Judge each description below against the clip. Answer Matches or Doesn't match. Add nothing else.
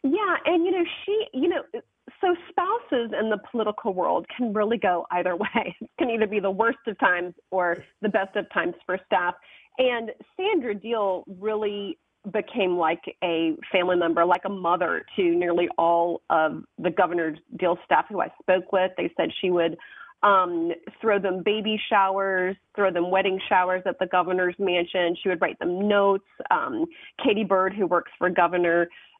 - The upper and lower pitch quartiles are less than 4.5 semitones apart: Matches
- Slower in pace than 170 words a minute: Doesn't match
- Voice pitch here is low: Doesn't match